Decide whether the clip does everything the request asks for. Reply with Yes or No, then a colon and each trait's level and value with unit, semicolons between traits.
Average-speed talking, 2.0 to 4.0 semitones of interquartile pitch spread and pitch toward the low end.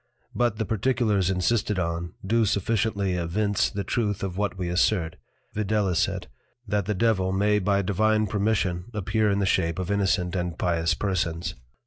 Yes: average, 155 wpm; average, 2.9 semitones; low, 100 Hz